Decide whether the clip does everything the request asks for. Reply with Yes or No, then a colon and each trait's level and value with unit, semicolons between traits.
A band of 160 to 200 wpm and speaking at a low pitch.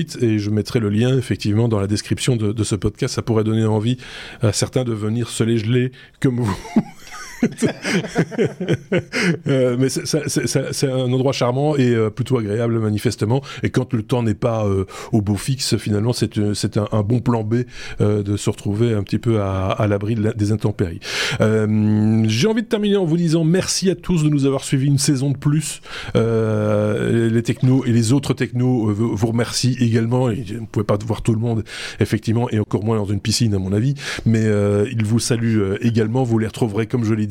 No: average, 215 wpm; low, 115 Hz